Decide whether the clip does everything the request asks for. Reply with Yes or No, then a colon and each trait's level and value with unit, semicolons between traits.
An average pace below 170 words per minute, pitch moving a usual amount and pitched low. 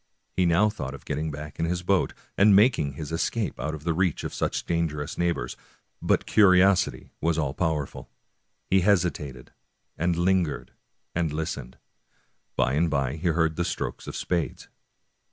Yes: average, 160 wpm; average, 3.3 semitones; very low, 85 Hz